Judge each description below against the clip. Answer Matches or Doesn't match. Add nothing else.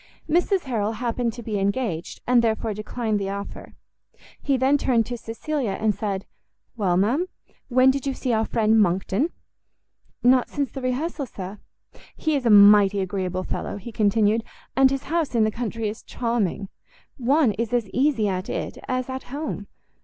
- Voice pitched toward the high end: Matches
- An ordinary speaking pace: Matches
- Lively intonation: Doesn't match